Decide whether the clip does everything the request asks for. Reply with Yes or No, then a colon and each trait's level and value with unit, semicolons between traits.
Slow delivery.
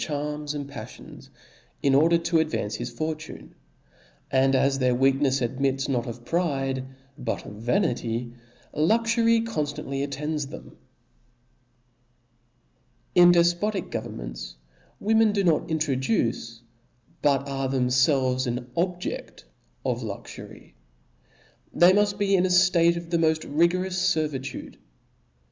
Yes: slow, 125 wpm